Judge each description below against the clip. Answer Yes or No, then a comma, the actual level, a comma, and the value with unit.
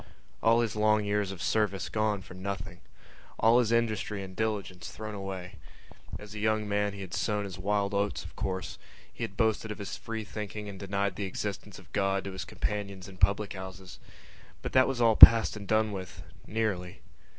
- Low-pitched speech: Yes, low, 100 Hz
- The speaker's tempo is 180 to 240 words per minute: Yes, average, 195 wpm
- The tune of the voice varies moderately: No, narrow, 2.0 semitones